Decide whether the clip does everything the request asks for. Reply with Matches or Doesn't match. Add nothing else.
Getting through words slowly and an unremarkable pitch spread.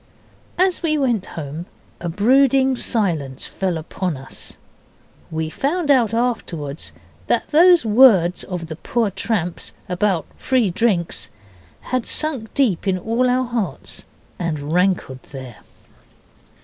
Doesn't match